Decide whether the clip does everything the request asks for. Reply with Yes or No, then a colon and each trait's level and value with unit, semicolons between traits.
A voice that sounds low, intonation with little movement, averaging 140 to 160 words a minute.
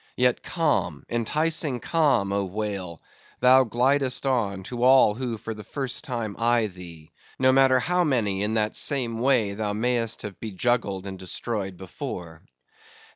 No: low, 115 Hz; average, 4.5 semitones; average, 150 wpm